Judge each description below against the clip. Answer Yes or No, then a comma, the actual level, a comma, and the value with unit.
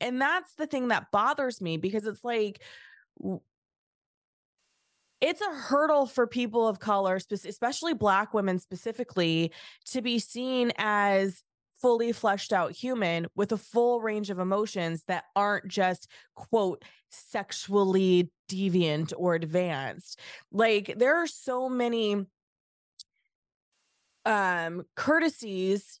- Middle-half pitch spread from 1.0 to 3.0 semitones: No, average, 4.5 semitones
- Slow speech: Yes, slow, 115 wpm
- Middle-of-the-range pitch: No, high, 210 Hz